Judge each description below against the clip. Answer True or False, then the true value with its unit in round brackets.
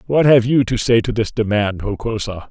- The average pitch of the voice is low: True (115 Hz)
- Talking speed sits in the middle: False (215 wpm)